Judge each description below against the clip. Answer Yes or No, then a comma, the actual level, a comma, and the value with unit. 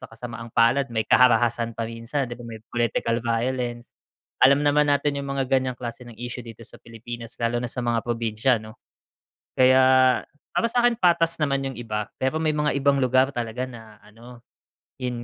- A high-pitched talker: No, low, 120 Hz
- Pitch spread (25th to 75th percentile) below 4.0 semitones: Yes, narrow, 2.6 semitones